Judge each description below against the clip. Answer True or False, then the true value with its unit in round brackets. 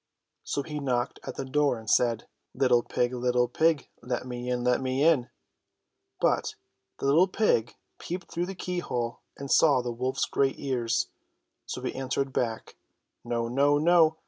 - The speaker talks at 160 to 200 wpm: True (170 wpm)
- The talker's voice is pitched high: False (130 Hz)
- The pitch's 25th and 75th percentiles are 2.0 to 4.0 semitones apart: True (3.3 semitones)